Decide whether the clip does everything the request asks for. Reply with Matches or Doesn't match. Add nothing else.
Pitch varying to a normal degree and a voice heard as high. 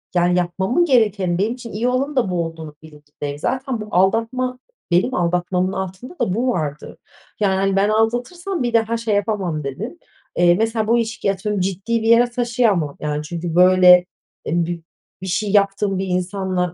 Matches